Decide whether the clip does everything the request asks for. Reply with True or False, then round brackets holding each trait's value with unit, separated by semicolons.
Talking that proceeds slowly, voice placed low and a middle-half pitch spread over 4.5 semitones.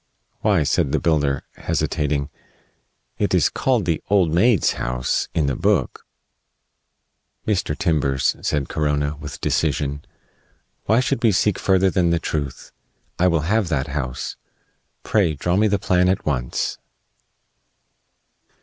True (130 wpm; 80 Hz; 5.0 semitones)